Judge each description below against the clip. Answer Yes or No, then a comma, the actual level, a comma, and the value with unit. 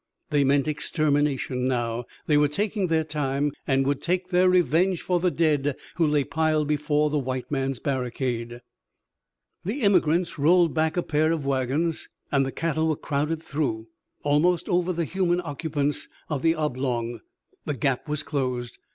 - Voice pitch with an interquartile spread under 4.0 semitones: Yes, average, 3.4 semitones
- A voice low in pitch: No, medium, 150 Hz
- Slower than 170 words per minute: Yes, average, 160 wpm